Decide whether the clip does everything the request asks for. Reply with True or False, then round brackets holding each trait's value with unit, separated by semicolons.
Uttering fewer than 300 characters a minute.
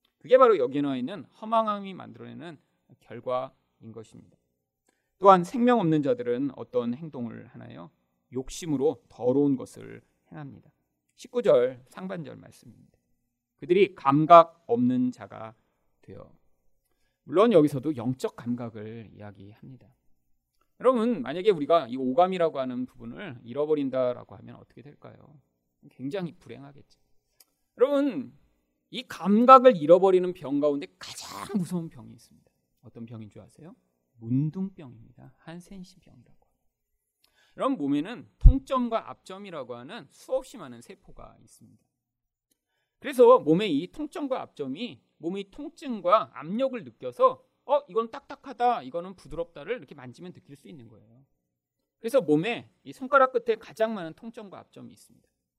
False (310 characters per minute)